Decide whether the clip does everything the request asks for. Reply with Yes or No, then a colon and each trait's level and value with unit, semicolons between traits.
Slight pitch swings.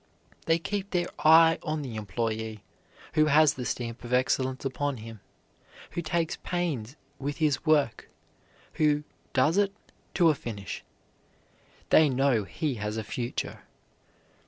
No: average, 5.2 semitones